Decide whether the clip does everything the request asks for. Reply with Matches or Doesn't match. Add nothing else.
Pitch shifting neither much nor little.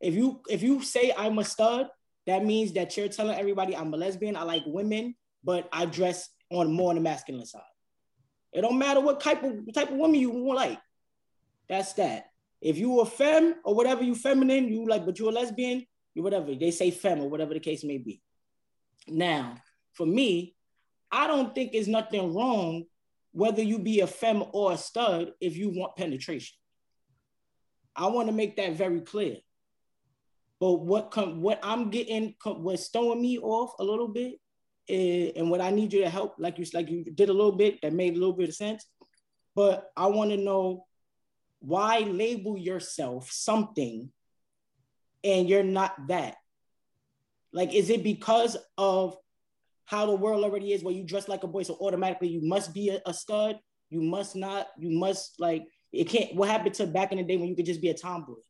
Matches